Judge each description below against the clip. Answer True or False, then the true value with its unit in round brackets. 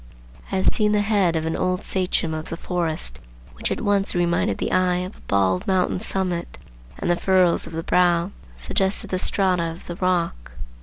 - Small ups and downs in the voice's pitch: True (2.2 semitones)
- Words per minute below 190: False (195 wpm)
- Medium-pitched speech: True (180 Hz)